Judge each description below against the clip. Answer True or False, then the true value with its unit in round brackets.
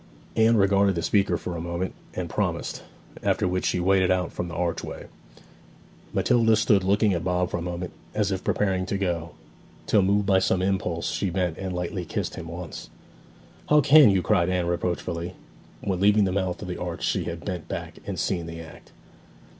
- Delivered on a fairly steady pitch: True (2.2 semitones)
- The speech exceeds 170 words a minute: True (195 wpm)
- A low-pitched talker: True (90 Hz)